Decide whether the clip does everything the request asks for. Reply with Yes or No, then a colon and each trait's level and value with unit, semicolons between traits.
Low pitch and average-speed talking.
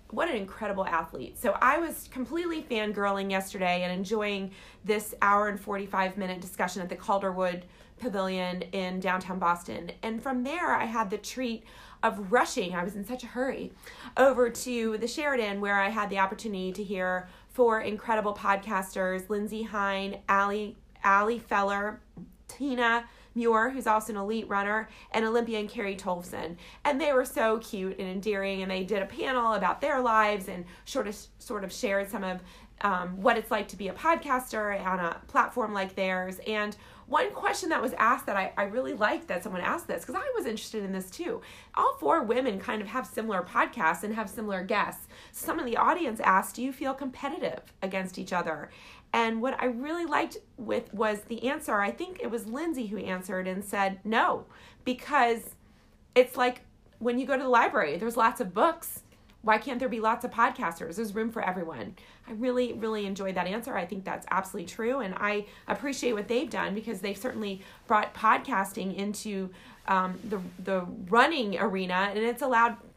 No: high, 215 Hz; average, 185 wpm